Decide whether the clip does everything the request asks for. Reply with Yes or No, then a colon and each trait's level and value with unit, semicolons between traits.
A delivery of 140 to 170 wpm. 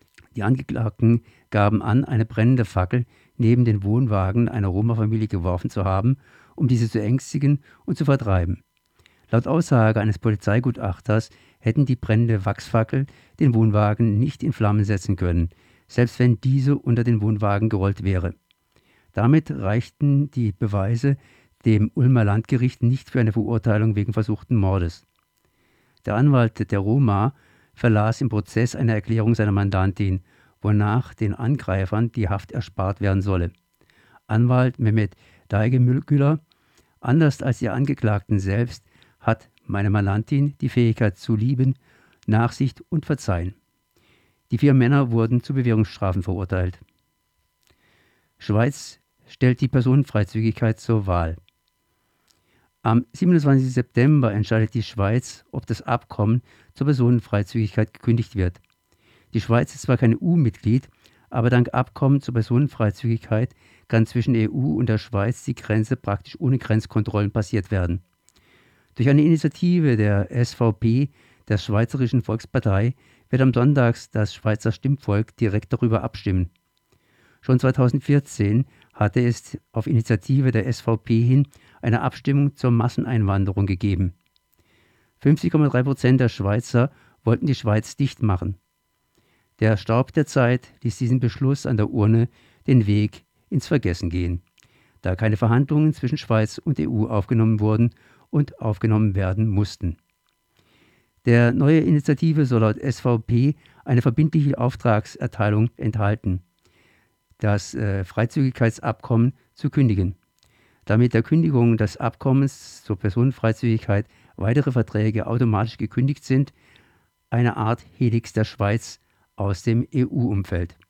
No: slow, 125 wpm